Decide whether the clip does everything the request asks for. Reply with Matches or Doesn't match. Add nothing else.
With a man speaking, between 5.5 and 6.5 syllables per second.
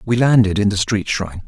Matches